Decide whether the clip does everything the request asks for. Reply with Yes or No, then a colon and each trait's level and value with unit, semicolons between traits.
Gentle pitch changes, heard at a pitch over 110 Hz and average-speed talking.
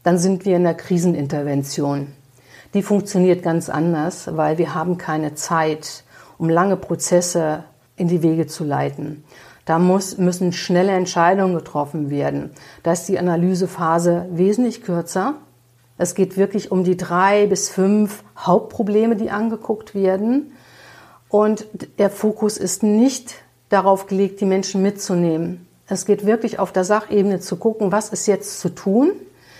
No: average, 3.4 semitones; medium, 185 Hz; average, 145 wpm